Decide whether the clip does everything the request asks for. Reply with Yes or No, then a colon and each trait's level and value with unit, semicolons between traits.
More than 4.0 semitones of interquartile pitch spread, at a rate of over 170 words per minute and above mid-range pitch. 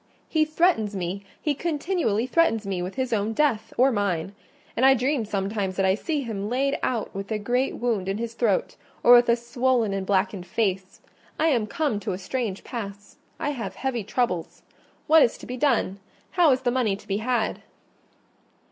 Yes: average, 4.7 semitones; average, 190 wpm; high, 225 Hz